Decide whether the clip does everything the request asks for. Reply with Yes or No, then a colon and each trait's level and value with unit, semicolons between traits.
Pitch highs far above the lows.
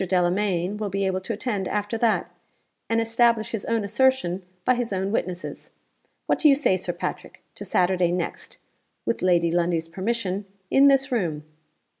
No: average, 4.2 semitones